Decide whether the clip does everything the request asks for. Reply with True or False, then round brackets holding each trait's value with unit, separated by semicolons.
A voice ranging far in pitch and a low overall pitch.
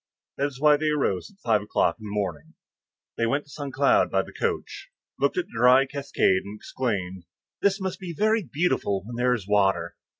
True (6.8 semitones; 125 Hz)